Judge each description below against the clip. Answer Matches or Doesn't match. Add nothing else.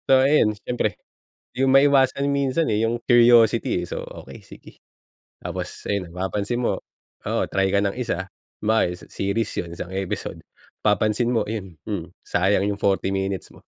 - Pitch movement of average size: Matches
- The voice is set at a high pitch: Doesn't match